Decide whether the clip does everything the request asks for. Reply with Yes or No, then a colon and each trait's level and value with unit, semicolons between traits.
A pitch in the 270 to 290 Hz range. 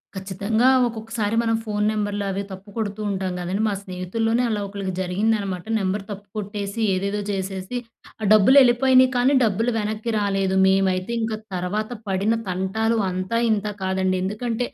No: high, 205 Hz